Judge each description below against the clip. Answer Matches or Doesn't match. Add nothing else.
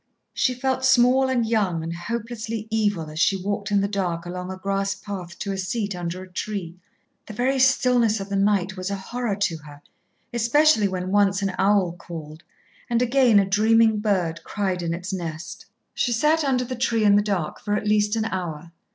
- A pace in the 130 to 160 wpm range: Doesn't match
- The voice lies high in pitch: Matches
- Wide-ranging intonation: Doesn't match